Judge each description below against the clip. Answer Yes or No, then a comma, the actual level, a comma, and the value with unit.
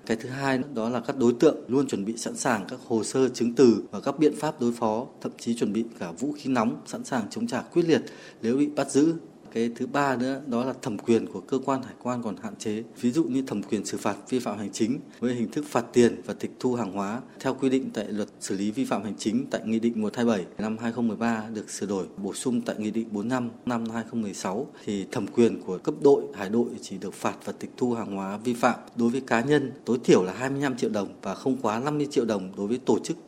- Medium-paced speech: No, fast, 260 wpm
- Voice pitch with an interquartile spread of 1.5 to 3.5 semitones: Yes, average, 2.9 semitones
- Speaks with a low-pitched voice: Yes, low, 120 Hz